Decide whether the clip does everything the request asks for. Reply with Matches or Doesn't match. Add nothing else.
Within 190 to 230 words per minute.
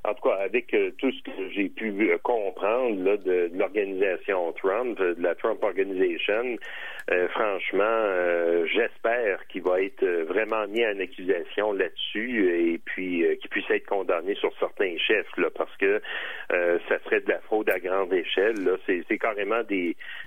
Doesn't match